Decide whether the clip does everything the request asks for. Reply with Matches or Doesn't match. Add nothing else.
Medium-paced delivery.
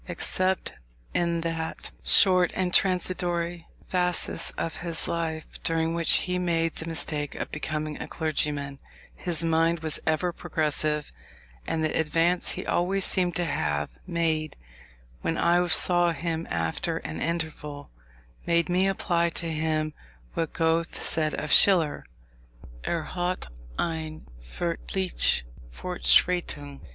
Doesn't match